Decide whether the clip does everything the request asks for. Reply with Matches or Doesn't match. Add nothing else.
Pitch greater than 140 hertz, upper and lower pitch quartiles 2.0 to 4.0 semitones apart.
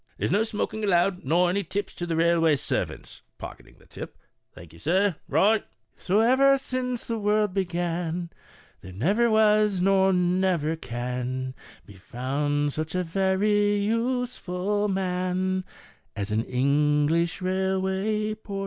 Doesn't match